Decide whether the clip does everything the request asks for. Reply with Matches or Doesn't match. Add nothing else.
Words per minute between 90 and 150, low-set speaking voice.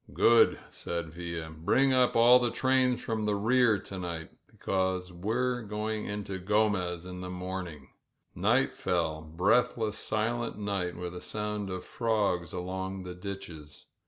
Matches